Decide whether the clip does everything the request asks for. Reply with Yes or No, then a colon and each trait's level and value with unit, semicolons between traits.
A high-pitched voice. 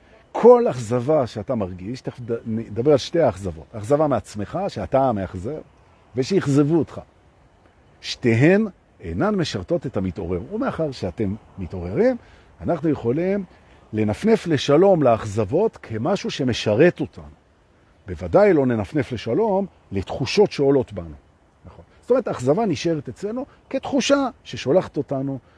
No: low, 135 Hz